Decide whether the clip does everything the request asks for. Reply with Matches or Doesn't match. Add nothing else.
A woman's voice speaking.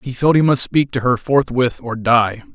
Doesn't match